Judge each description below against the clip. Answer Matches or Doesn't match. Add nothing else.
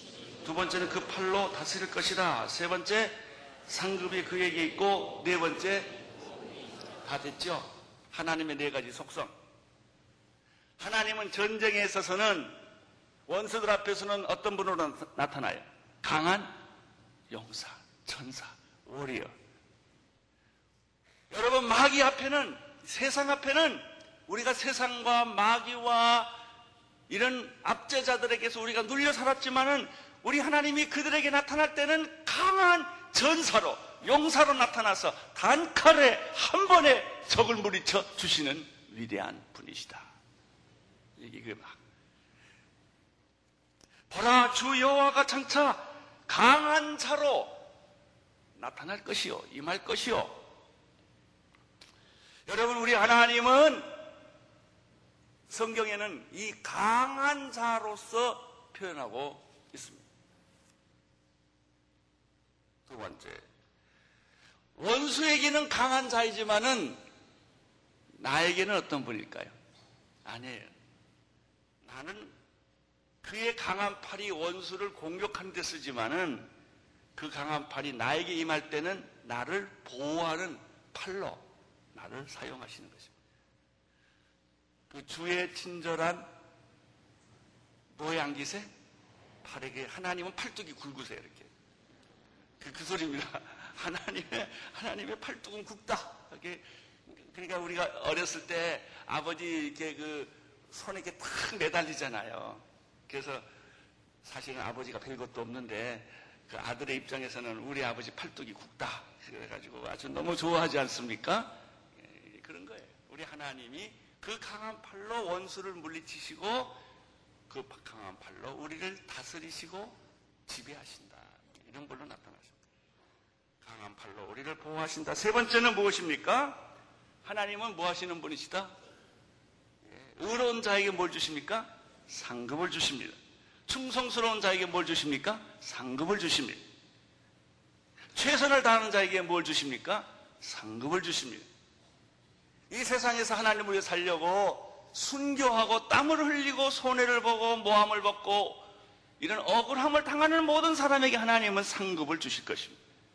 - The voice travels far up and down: Matches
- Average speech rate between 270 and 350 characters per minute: Doesn't match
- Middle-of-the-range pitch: Doesn't match